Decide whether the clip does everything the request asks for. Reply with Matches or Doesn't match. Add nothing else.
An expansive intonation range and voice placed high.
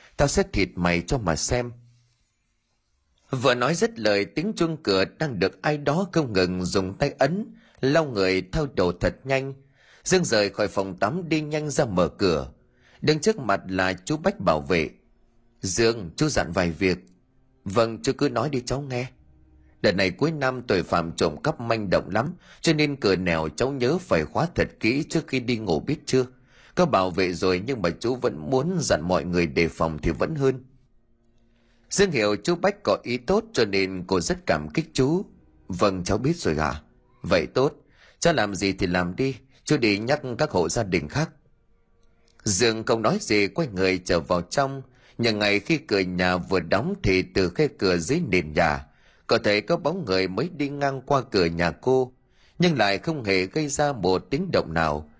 Doesn't match